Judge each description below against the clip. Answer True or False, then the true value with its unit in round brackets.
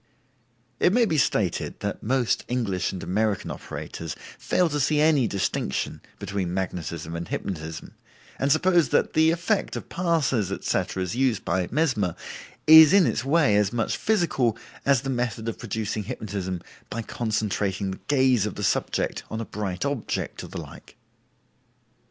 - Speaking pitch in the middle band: False (115 Hz)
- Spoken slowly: False (155 wpm)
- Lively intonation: True (7.0 semitones)